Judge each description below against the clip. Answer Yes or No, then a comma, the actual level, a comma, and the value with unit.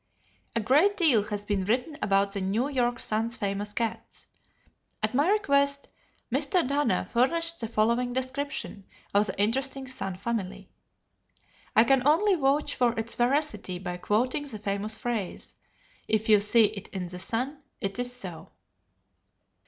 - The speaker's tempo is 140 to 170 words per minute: Yes, average, 150 wpm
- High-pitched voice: Yes, high, 235 Hz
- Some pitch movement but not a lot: Yes, average, 5.0 semitones